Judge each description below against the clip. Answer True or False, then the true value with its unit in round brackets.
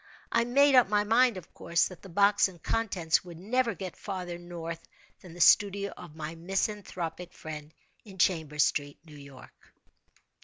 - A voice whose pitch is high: False (180 Hz)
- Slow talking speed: False (165 wpm)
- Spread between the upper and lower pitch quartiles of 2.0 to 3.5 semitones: False (4.0 semitones)